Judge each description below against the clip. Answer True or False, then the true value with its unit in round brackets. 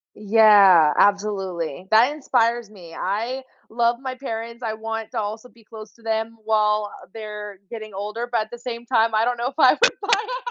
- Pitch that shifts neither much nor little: False (2.2 semitones)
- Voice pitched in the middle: False (225 Hz)